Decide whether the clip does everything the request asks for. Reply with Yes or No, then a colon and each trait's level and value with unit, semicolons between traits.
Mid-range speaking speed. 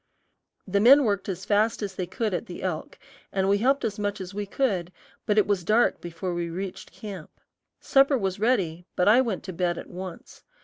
No: fast, 210 wpm